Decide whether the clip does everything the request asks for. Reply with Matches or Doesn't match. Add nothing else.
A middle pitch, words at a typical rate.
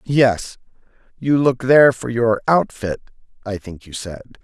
Doesn't match